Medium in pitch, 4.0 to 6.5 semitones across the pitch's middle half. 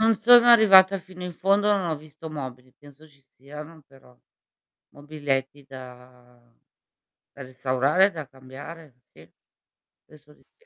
Yes: medium, 150 Hz; wide, 5.4 semitones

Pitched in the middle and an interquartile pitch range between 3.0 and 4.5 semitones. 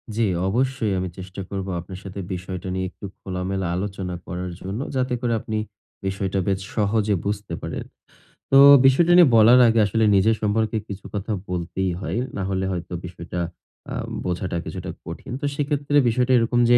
No: low, 100 Hz; average, 3.6 semitones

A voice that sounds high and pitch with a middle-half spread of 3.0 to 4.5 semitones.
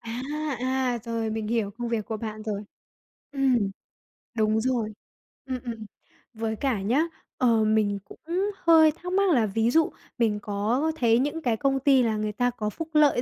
Yes: high, 235 Hz; average, 3.5 semitones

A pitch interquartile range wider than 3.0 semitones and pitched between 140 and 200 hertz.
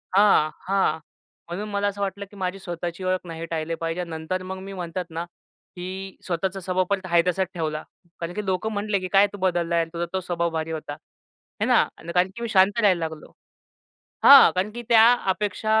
No: average, 2.7 semitones; medium, 185 Hz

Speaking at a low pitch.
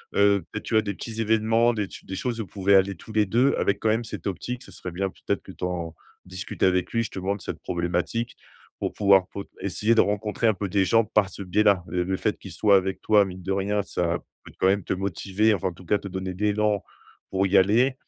Yes: low, 100 Hz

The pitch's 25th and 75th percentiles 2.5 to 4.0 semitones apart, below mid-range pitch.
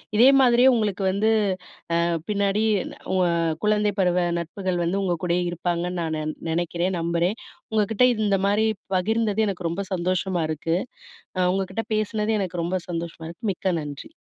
No: average, 3.5 semitones; medium, 185 Hz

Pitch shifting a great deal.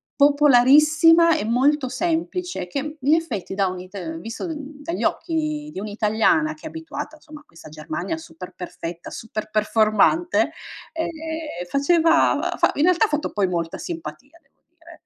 Yes: wide, 7.2 semitones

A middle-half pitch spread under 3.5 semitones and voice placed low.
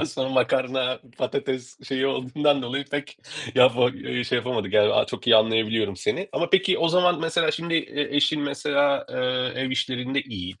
Yes: average, 2.7 semitones; low, 130 Hz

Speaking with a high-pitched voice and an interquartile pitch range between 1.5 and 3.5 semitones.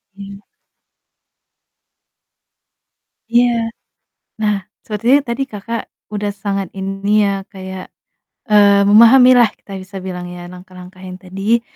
Yes: high, 200 Hz; average, 3.1 semitones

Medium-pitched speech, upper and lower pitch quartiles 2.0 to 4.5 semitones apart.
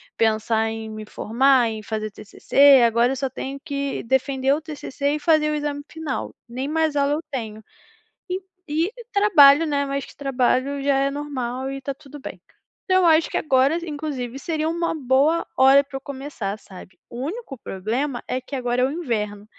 No: very high, 275 Hz; average, 3.4 semitones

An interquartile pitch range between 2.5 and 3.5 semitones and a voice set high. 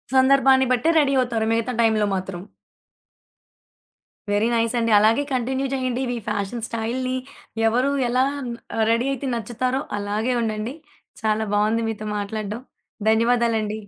Yes: average, 2.8 semitones; high, 230 Hz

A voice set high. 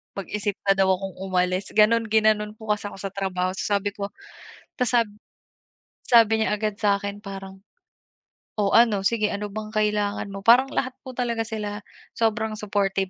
Yes: high, 210 Hz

